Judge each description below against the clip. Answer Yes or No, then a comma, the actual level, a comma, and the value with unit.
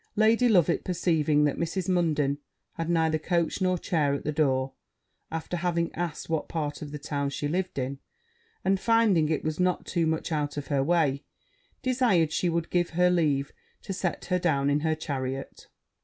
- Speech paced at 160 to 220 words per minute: Yes, average, 180 wpm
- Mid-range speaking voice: Yes, medium, 160 Hz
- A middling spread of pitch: Yes, average, 3.3 semitones